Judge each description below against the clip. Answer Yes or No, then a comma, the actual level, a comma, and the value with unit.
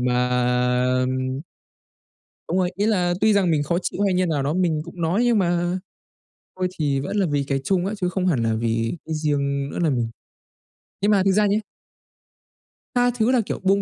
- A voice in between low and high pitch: Yes, medium, 175 Hz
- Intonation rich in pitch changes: Yes, wide, 5.8 semitones